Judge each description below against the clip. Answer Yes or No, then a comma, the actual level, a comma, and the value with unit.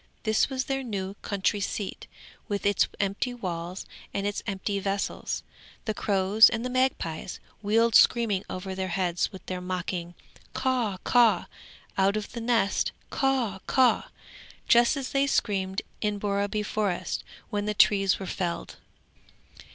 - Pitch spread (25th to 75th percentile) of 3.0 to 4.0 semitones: Yes, average, 3.4 semitones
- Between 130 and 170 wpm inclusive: Yes, average, 145 wpm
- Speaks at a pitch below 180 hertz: No, high, 205 Hz